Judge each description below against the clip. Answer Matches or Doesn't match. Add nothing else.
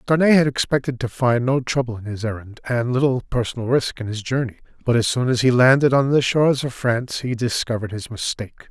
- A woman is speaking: Doesn't match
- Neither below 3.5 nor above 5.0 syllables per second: Doesn't match